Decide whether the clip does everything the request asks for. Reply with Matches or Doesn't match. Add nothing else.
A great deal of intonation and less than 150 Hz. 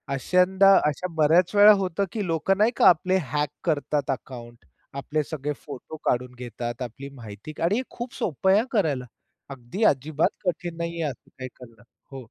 Doesn't match